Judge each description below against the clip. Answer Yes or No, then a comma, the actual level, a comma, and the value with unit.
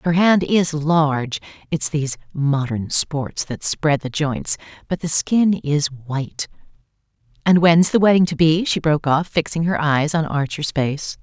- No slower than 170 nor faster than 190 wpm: No, average, 155 wpm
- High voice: No, medium, 155 Hz